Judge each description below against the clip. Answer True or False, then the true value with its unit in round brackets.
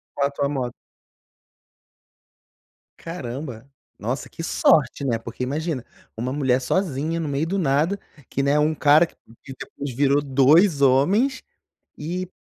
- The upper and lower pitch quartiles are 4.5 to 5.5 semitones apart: False (3.6 semitones)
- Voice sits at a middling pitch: True (145 Hz)